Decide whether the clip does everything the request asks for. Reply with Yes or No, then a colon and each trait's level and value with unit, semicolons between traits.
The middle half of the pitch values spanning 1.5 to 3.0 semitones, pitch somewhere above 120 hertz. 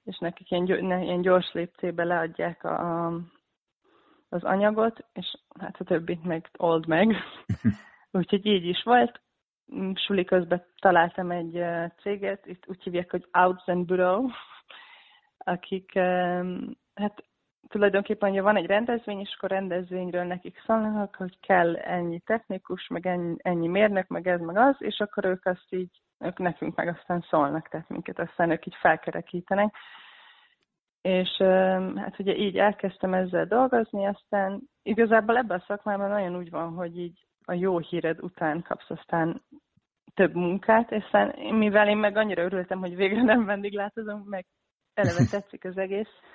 Yes: average, 2.7 semitones; medium, 185 Hz